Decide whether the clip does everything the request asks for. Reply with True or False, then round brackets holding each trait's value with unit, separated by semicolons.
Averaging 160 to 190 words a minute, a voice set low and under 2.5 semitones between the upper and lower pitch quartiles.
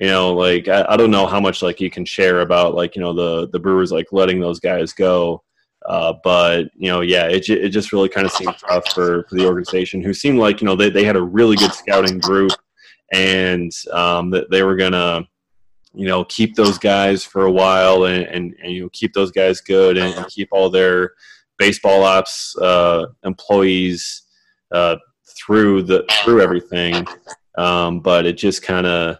False (200 wpm; 95 Hz; 1.6 semitones)